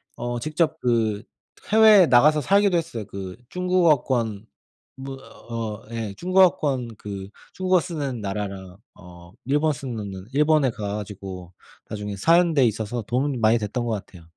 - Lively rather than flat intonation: Yes, wide, 6.8 semitones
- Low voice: Yes, low, 120 Hz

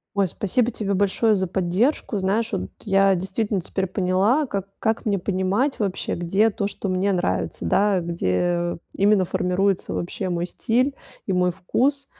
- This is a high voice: Yes, high, 195 Hz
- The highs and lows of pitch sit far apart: No, average, 2.7 semitones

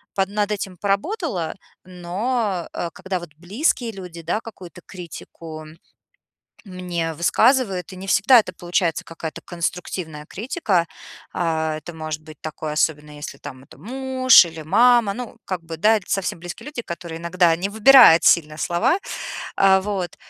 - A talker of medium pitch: Yes, medium, 180 Hz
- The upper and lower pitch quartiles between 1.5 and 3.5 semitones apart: No, average, 4.2 semitones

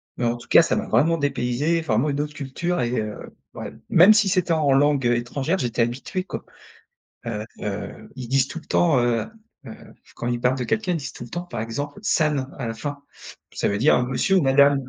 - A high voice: No, low, 135 Hz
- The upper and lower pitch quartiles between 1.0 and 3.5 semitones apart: No, average, 5.0 semitones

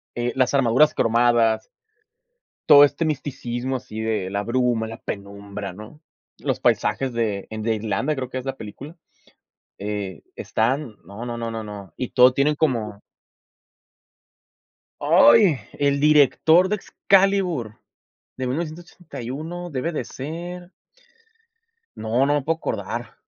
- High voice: No, low, 125 Hz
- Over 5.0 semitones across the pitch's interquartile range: Yes, wide, 5.4 semitones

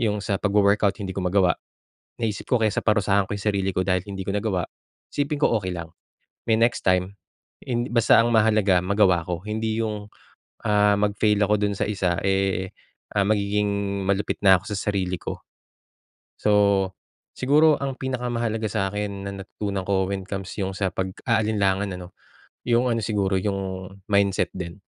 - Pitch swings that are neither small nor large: No, narrow, 2.0 semitones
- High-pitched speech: No, low, 100 Hz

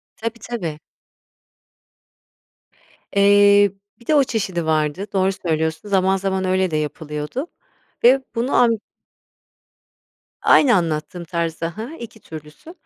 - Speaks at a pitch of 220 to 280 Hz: No, high, 190 Hz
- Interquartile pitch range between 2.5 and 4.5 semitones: No, wide, 5.6 semitones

